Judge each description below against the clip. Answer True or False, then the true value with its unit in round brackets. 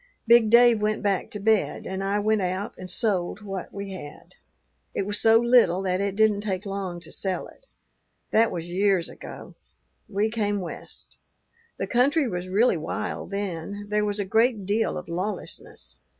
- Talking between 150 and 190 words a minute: True (175 wpm)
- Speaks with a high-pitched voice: True (205 Hz)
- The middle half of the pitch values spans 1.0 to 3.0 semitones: True (2.6 semitones)